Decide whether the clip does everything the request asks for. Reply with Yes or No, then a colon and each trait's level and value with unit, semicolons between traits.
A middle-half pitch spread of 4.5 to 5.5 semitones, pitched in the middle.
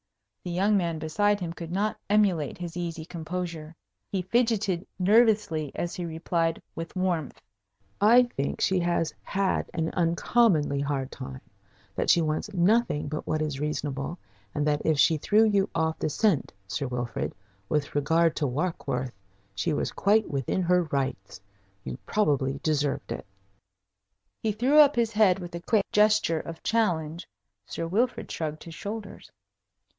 Yes: average, 5.0 semitones; medium, 170 Hz